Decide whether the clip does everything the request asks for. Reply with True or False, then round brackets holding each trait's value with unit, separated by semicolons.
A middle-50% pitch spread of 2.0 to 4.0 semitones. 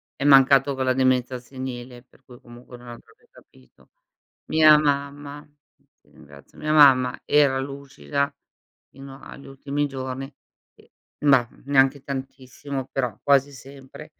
False (1.6 semitones)